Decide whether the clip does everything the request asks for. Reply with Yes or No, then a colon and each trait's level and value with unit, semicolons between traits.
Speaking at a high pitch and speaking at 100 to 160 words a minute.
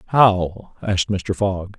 No: low, 100 Hz; slow, 135 wpm